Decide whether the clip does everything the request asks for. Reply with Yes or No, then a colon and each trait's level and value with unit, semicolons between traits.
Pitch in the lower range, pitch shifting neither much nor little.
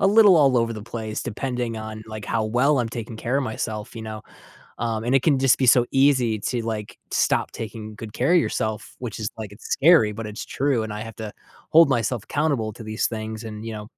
Yes: low, 115 Hz; average, 3.1 semitones